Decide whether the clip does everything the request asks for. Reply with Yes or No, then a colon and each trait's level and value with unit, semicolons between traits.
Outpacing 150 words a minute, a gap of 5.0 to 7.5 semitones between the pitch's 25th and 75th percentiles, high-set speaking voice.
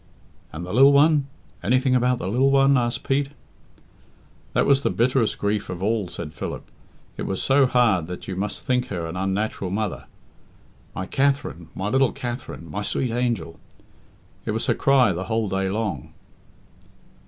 No: average, 165 wpm; wide, 5.4 semitones; low, 110 Hz